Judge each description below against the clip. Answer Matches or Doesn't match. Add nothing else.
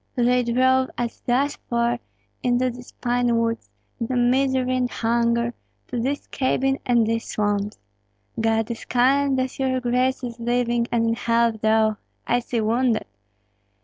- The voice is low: Doesn't match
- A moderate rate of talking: Matches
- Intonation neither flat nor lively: Doesn't match